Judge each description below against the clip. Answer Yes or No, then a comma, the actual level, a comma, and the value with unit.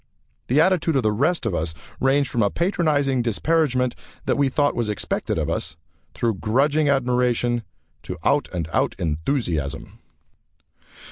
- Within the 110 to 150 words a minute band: Yes, average, 145 wpm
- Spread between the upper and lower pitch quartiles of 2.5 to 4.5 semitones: No, average, 4.9 semitones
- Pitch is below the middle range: Yes, low, 125 Hz